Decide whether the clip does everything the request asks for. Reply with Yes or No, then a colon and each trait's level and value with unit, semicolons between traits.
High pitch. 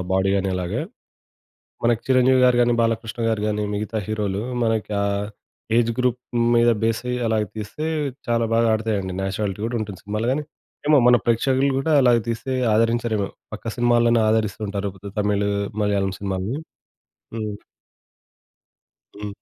No: low, 110 Hz